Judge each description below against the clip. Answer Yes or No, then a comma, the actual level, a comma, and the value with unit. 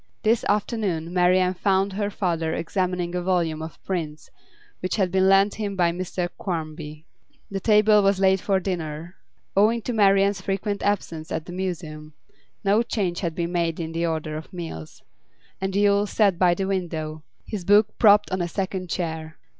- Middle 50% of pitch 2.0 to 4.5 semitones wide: Yes, average, 3.1 semitones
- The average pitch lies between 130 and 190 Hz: Yes, medium, 185 Hz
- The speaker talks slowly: No, average, 170 wpm